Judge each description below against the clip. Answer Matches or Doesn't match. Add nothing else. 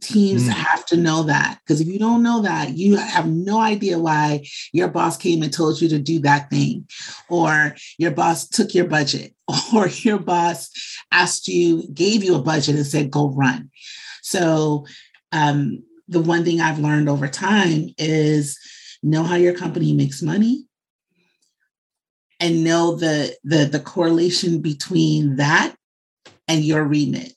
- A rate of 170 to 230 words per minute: Doesn't match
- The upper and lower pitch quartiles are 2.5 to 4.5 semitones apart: Matches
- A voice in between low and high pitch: Matches